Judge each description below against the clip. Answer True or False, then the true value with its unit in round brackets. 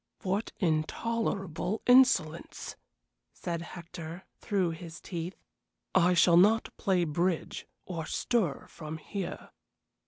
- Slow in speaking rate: True (100 wpm)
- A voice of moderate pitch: True (175 Hz)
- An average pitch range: True (3.3 semitones)